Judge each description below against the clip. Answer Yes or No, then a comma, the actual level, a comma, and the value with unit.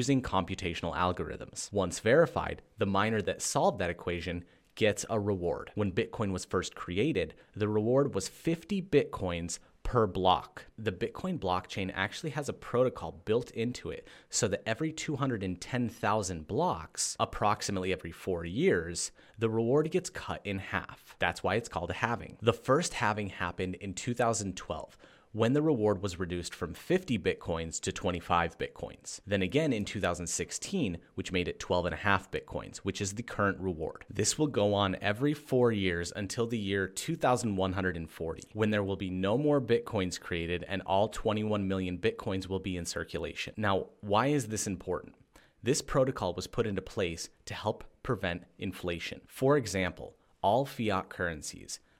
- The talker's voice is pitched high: No, low, 100 Hz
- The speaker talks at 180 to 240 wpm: No, average, 155 wpm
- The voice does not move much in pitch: No, average, 4.3 semitones